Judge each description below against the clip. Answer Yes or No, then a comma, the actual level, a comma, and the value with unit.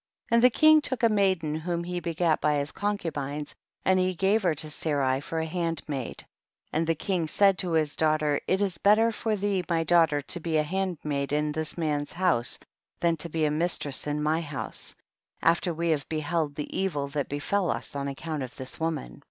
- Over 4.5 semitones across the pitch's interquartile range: No, average, 3.6 semitones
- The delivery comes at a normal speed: No, fast, 215 wpm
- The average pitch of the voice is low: No, medium, 160 Hz